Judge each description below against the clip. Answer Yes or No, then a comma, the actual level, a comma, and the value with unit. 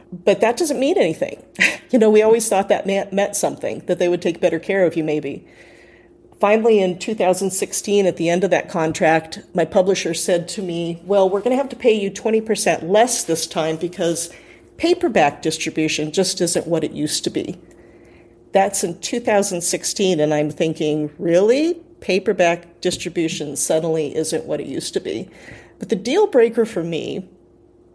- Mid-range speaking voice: Yes, medium, 180 Hz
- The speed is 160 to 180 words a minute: Yes, average, 170 wpm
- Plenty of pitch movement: No, average, 4.0 semitones